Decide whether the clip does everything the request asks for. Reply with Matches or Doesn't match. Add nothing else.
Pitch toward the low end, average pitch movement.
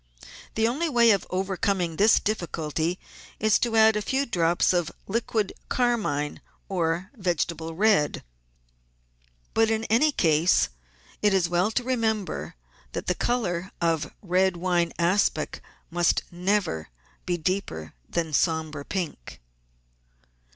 Doesn't match